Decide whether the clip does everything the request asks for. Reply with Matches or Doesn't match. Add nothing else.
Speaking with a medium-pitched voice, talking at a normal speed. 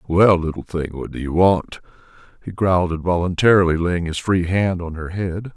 Doesn't match